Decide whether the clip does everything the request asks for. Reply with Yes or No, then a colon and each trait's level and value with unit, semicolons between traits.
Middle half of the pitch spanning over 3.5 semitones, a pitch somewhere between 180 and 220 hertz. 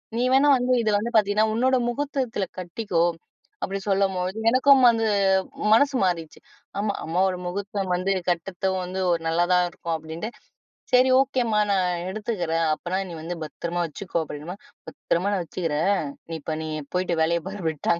Yes: average, 4.2 semitones; high, 190 Hz